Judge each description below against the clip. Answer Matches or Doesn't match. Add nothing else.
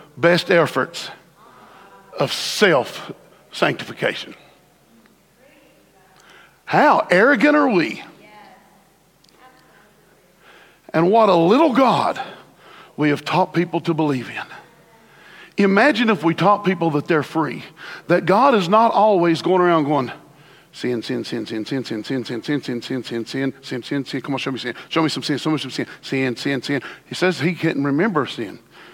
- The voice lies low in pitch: Doesn't match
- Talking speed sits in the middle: Matches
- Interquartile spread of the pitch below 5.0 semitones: Doesn't match